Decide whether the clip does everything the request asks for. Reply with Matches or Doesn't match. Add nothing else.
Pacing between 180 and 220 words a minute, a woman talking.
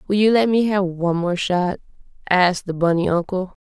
Matches